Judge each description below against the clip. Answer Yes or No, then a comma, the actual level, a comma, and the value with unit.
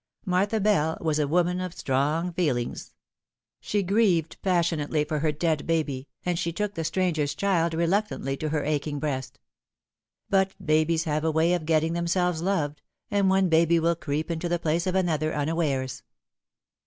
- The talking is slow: No, average, 165 wpm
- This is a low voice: No, medium, 165 Hz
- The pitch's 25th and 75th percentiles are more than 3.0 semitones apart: No, average, 2.7 semitones